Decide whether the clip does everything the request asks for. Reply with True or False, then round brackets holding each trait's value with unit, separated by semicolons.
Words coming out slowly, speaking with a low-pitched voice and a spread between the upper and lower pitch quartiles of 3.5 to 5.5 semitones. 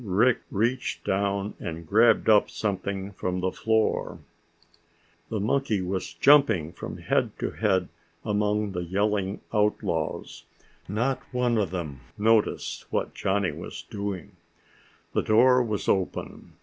False (125 wpm; 105 Hz; 2.9 semitones)